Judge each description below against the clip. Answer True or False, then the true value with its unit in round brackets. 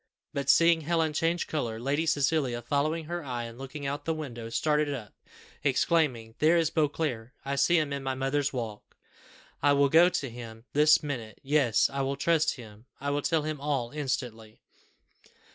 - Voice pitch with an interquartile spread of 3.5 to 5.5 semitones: True (4.0 semitones)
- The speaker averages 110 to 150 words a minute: False (180 wpm)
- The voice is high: False (140 Hz)